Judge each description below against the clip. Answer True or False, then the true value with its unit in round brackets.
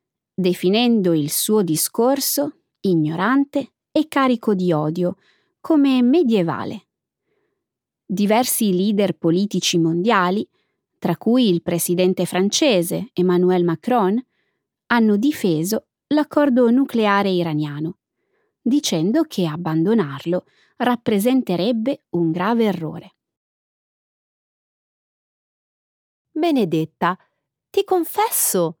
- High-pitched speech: True (200 Hz)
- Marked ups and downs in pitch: True (6.4 semitones)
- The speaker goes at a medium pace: False (75 wpm)